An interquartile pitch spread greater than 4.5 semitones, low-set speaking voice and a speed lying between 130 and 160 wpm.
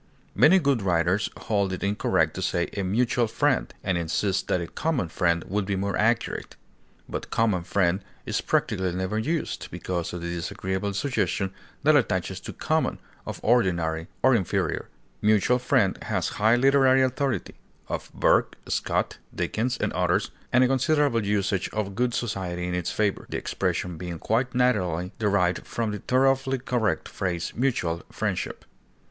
Yes: wide, 5.4 semitones; low, 100 Hz; average, 155 wpm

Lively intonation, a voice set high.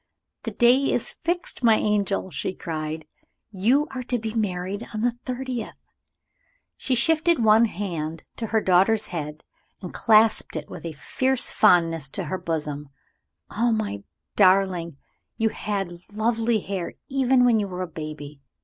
Yes: wide, 5.7 semitones; high, 205 Hz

